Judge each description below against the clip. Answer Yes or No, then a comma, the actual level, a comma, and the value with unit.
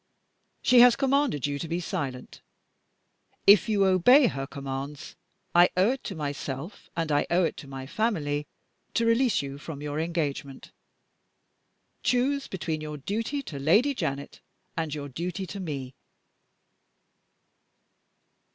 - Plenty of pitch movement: Yes, wide, 7.2 semitones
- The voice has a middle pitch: Yes, medium, 165 Hz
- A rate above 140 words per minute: No, slow, 135 wpm